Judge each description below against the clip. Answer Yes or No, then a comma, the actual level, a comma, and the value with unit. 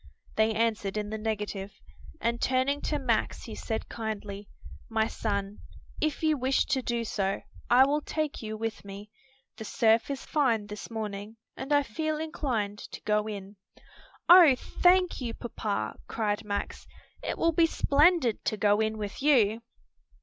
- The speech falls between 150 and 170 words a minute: Yes, average, 160 wpm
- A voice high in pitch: Yes, high, 225 Hz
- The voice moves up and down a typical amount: Yes, average, 4.8 semitones